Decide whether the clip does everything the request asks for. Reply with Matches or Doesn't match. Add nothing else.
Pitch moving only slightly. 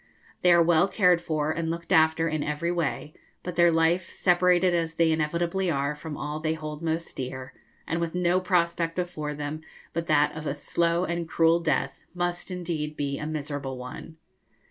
Matches